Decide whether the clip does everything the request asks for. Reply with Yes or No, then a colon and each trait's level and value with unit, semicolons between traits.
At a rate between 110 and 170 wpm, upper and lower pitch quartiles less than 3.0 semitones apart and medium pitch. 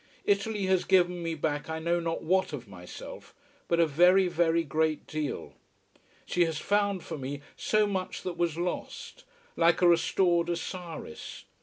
Yes: average, 160 wpm; narrow, 2.5 semitones; medium, 170 Hz